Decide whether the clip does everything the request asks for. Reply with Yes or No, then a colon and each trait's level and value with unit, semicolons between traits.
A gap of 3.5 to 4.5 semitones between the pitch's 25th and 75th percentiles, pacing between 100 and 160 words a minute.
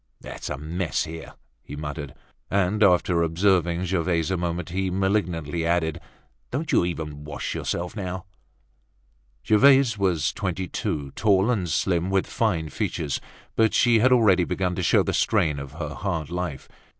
No: average, 3.1 semitones; average, 155 wpm